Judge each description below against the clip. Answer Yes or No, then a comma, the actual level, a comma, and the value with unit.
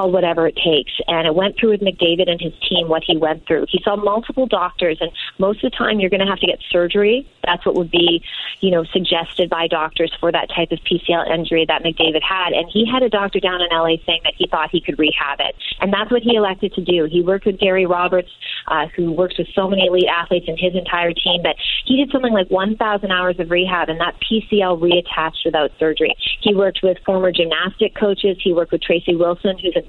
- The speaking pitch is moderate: Yes, medium, 180 Hz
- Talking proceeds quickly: Yes, fast, 235 wpm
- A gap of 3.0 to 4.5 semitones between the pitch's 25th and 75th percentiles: No, narrow, 2.6 semitones